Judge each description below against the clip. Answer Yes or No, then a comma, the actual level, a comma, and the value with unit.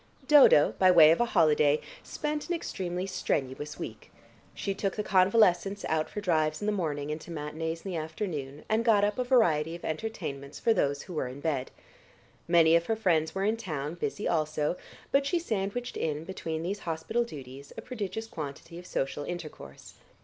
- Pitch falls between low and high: Yes, medium, 170 Hz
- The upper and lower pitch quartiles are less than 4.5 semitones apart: No, average, 5.2 semitones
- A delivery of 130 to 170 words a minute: No, average, 185 wpm